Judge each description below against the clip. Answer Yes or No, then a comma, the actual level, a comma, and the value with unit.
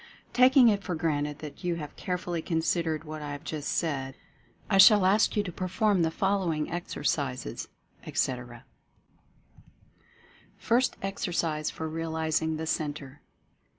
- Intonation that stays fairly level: No, average, 3.6 semitones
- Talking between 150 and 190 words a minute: No, slow, 135 wpm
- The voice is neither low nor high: Yes, medium, 160 Hz